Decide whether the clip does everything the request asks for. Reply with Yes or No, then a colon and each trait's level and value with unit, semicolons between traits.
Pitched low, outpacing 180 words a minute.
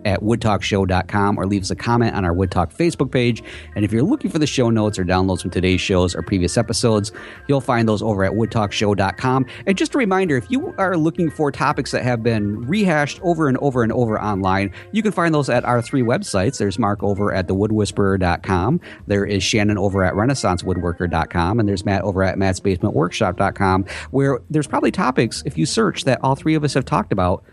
Yes: low, 105 Hz; fast, 205 wpm